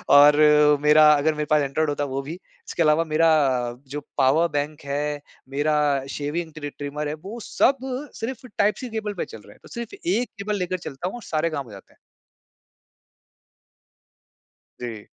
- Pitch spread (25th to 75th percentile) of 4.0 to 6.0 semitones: Yes, average, 4.4 semitones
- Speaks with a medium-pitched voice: Yes, medium, 155 Hz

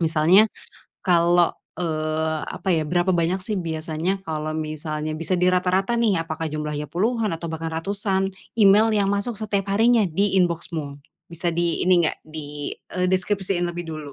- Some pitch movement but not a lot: Yes, average, 3.4 semitones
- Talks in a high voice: No, medium, 175 Hz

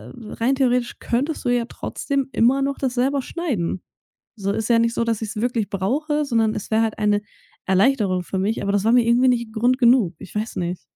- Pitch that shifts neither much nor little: Yes, average, 3.5 semitones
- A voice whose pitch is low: No, high, 230 Hz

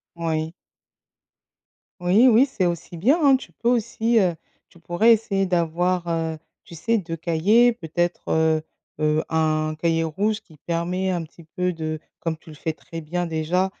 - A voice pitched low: No, medium, 170 Hz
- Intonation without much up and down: No, average, 3.3 semitones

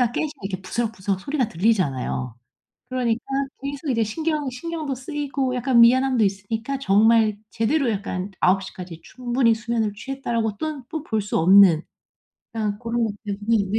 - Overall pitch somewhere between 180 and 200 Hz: No, high, 230 Hz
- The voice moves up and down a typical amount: Yes, average, 4.6 semitones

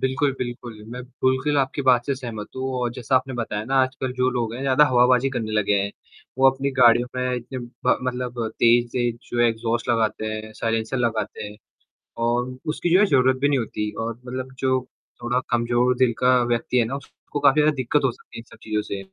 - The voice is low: Yes, low, 125 Hz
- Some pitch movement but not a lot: No, narrow, 2.0 semitones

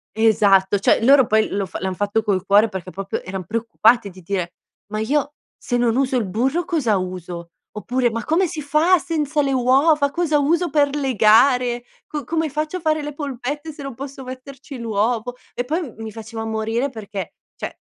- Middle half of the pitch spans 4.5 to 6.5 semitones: Yes, average, 5.3 semitones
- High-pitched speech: Yes, high, 245 Hz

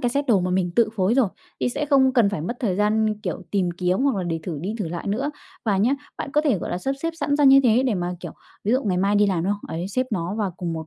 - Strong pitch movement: Yes, wide, 5.8 semitones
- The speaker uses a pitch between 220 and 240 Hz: No, high, 205 Hz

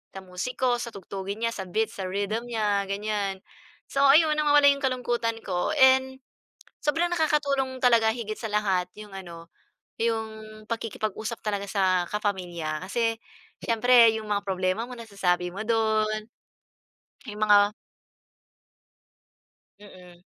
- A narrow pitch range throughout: No, average, 3.3 semitones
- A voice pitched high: Yes, high, 215 Hz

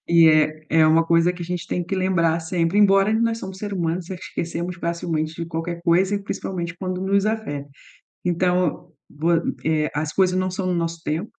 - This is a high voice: No, medium, 175 Hz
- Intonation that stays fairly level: Yes, narrow, 2.3 semitones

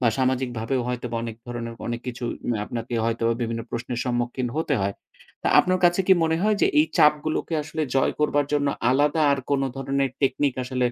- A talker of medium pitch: No, low, 130 Hz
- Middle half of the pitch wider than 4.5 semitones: No, average, 3.6 semitones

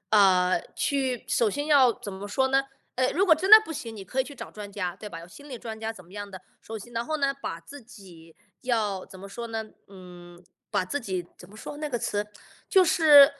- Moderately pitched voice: No, high, 220 Hz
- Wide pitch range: Yes, wide, 6.2 semitones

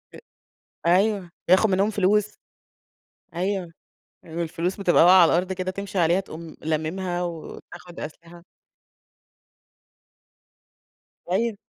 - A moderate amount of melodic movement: No, narrow, 2.3 semitones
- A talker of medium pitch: Yes, medium, 180 Hz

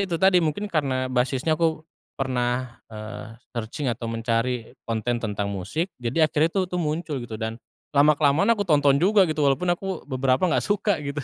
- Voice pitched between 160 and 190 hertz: No, medium, 140 Hz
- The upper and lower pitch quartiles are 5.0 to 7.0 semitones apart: Yes, average, 5.3 semitones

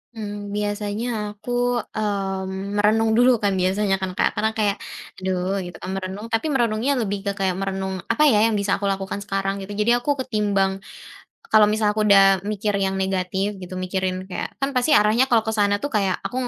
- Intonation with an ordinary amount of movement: No, narrow, 2.2 semitones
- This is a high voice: Yes, high, 205 Hz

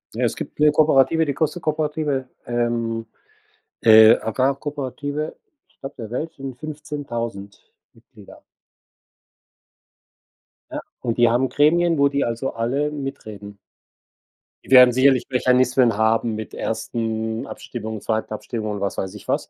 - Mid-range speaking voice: No, low, 125 Hz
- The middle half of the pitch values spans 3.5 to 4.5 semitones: Yes, average, 4.2 semitones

